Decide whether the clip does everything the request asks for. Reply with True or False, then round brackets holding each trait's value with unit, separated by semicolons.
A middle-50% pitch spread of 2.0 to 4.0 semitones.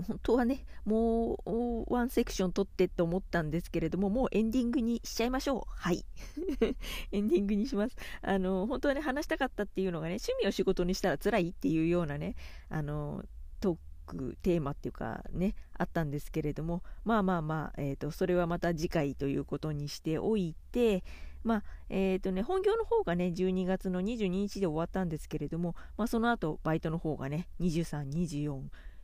False (5.4 semitones)